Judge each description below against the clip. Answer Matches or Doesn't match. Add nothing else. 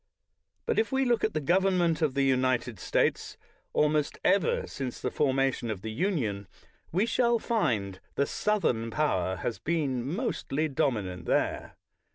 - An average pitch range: Doesn't match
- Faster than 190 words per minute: Doesn't match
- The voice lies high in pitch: Doesn't match